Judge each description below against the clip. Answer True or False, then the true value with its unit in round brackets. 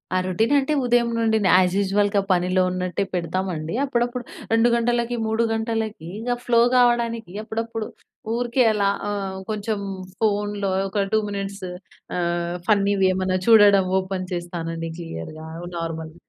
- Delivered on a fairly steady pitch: False (3.7 semitones)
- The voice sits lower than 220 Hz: True (200 Hz)